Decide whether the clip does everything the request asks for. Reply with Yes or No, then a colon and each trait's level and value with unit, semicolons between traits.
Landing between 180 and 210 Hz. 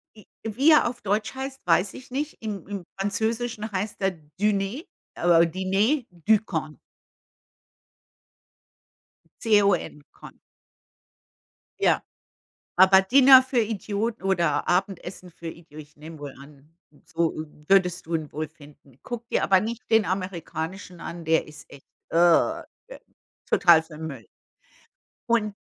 Yes: high, 190 Hz